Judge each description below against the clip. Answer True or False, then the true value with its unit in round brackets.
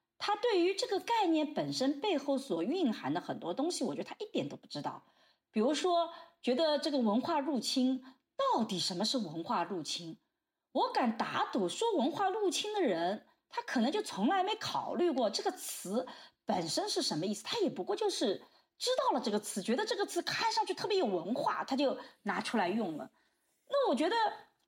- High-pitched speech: True (320 Hz)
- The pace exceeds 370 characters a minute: False (280 characters per minute)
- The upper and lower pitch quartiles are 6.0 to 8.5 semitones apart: True (7.1 semitones)